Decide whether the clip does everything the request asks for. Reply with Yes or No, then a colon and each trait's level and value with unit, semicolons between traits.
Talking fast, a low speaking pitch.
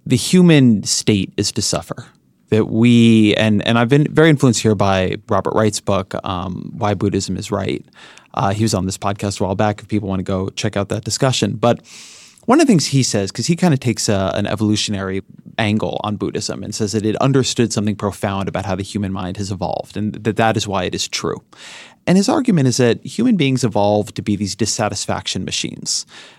Yes: fast, 215 wpm; low, 105 Hz